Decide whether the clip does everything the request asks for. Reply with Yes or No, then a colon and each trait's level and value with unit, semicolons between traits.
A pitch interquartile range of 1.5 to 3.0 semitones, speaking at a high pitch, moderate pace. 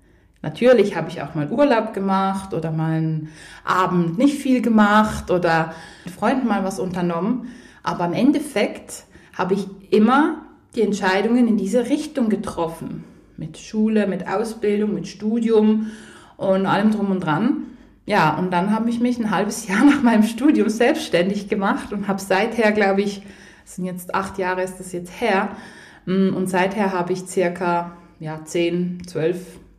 No: average, 3.6 semitones; high, 195 Hz; average, 160 wpm